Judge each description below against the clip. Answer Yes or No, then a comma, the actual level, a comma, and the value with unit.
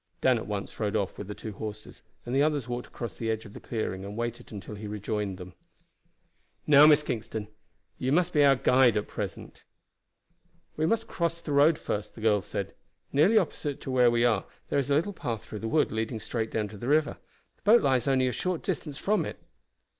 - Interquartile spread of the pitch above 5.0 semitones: Yes, wide, 5.5 semitones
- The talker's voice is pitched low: Yes, low, 120 Hz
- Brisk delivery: Yes, fast, 220 wpm